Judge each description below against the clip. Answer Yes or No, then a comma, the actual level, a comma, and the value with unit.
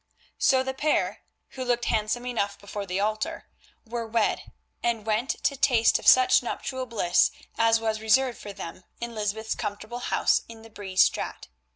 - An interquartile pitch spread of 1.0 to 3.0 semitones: Yes, narrow, 2.6 semitones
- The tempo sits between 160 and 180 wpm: Yes, average, 170 wpm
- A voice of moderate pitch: No, high, 225 Hz